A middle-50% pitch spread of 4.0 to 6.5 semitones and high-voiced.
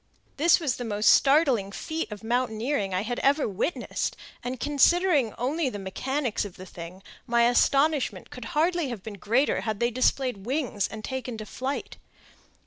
Yes: average, 4.8 semitones; high, 245 Hz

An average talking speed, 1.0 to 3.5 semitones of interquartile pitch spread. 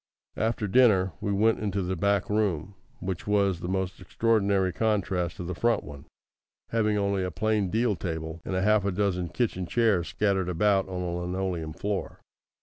Yes: average, 170 wpm; average, 2.7 semitones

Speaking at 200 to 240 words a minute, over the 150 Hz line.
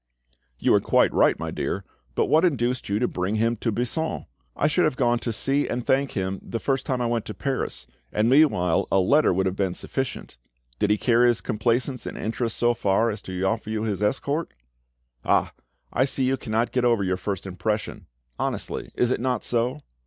No: fast, 205 wpm; low, 115 Hz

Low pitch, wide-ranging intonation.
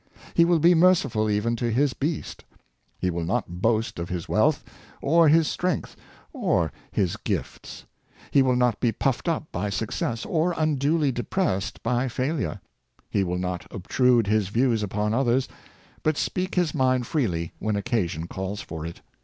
Yes: low, 120 Hz; wide, 6.6 semitones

